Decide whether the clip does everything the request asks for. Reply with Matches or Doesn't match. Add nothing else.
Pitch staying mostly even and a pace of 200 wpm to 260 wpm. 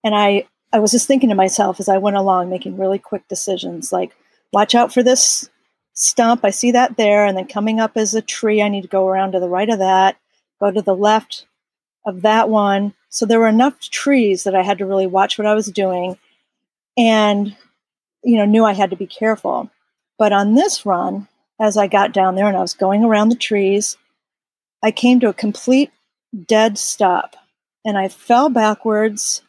Matches